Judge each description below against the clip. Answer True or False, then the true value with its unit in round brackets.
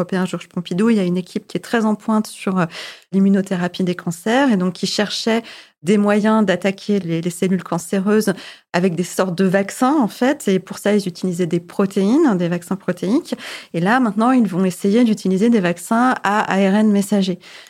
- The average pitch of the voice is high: True (195 Hz)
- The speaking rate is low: False (185 wpm)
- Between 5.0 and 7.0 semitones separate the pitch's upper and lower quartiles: False (3.0 semitones)